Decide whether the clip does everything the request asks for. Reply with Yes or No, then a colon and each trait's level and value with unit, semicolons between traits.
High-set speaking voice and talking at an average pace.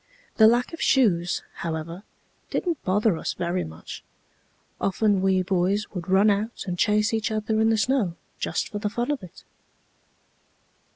Yes: high, 205 Hz; average, 160 wpm